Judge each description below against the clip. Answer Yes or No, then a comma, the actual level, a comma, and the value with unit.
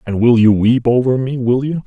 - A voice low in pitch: Yes, low, 120 Hz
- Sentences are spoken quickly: Yes, fast, 260 wpm